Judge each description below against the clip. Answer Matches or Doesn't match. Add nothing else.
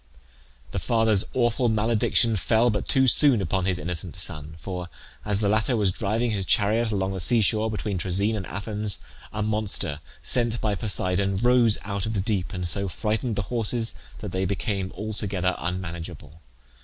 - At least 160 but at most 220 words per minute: Matches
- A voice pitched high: Doesn't match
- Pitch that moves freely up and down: Doesn't match